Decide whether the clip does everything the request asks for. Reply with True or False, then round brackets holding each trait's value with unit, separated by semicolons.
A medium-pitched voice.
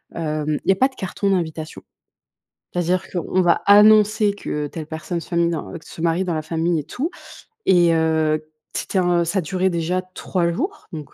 True (175 Hz)